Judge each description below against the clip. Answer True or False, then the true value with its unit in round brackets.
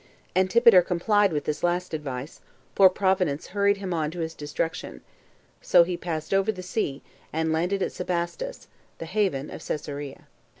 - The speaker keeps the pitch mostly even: False (3.6 semitones)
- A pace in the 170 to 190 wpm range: False (160 wpm)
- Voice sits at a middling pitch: True (175 Hz)